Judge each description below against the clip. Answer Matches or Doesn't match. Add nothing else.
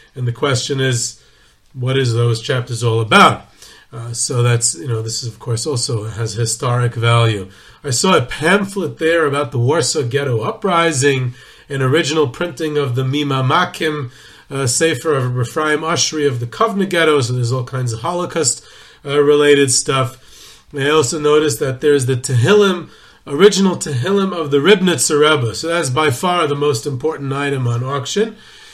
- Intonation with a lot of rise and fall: Doesn't match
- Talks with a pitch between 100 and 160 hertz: Matches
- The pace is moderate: Matches